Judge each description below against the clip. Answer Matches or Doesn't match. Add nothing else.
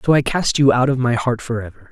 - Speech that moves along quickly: Matches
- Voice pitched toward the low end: Matches